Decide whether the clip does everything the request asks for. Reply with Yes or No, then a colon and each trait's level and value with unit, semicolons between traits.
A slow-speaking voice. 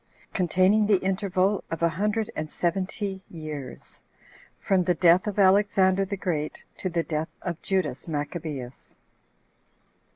Yes: slow, 125 wpm